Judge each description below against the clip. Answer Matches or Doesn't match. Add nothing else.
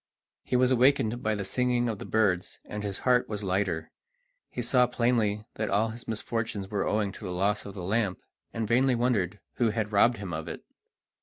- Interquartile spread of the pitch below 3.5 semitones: Matches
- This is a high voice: Doesn't match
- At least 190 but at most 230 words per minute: Matches